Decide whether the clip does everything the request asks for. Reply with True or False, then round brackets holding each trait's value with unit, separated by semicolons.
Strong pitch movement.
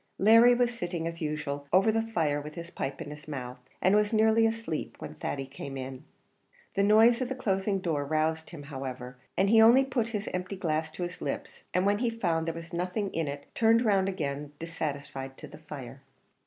True (6.8 semitones)